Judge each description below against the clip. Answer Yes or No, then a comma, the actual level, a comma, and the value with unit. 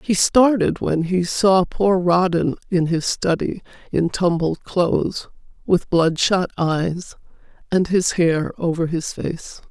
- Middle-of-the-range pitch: Yes, medium, 175 Hz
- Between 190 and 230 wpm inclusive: No, average, 140 wpm